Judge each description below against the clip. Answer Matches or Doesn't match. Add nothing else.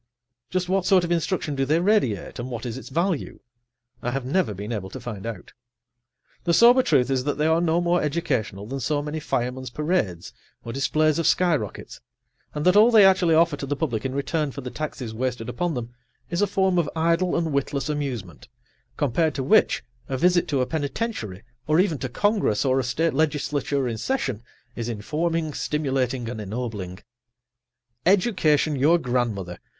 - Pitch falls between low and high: Matches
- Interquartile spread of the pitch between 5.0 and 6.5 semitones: Matches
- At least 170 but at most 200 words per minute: Matches